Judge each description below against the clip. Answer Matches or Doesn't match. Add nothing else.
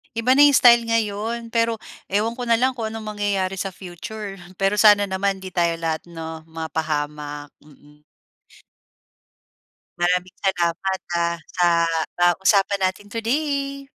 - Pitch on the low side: Doesn't match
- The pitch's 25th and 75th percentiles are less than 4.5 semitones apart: Doesn't match